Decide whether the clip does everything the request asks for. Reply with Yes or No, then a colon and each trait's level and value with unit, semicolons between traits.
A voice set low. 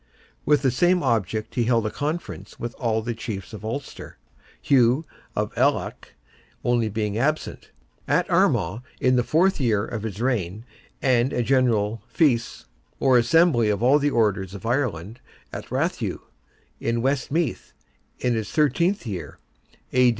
Yes: low, 120 Hz